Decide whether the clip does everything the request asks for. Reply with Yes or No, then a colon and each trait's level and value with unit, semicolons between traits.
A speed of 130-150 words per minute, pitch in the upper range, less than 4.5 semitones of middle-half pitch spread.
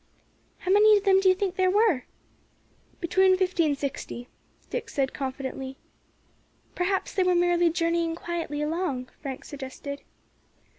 No: average, 140 wpm; very high, 340 Hz; average, 4.9 semitones